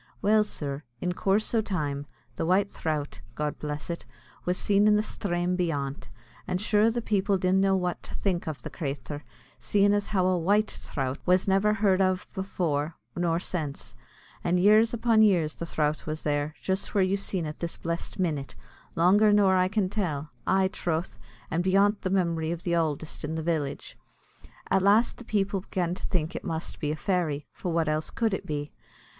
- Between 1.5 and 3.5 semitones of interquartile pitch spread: No, average, 4.1 semitones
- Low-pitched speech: No, medium, 180 Hz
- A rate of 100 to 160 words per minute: No, average, 195 wpm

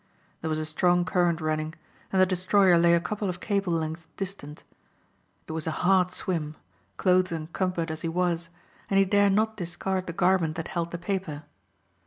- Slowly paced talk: No, average, 185 wpm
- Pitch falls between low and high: Yes, medium, 175 Hz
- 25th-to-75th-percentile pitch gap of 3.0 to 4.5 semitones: No, narrow, 2.6 semitones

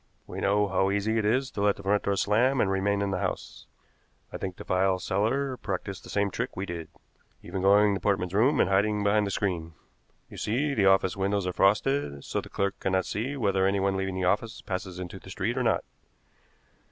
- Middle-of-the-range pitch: No, low, 100 Hz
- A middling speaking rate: No, fast, 220 wpm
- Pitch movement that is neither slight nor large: No, narrow, 1.9 semitones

